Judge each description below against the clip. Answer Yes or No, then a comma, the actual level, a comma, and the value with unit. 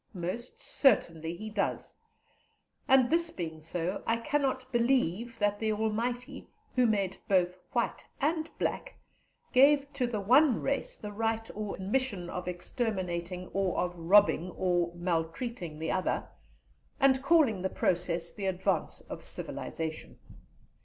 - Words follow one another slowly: Yes, slow, 130 wpm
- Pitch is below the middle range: No, high, 205 Hz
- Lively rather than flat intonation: Yes, wide, 6.0 semitones